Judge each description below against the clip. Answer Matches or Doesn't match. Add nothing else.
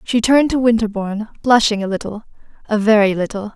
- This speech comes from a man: Doesn't match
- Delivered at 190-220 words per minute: Doesn't match